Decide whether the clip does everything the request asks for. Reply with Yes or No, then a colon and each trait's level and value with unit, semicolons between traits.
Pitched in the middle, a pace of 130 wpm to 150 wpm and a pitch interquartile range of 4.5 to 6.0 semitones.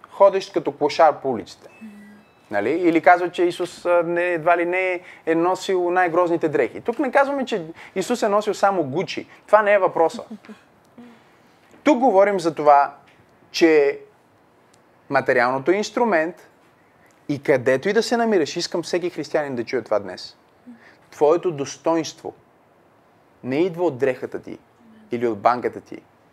Yes: medium, 180 Hz; average, 140 wpm; average, 4.8 semitones